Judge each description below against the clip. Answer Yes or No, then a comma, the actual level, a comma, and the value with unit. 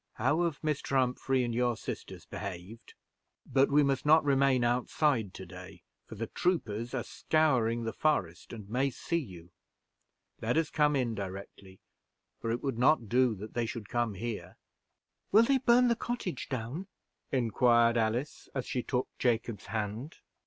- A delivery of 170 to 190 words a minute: No, average, 160 wpm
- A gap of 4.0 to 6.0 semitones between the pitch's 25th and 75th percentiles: Yes, average, 4.3 semitones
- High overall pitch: No, low, 120 Hz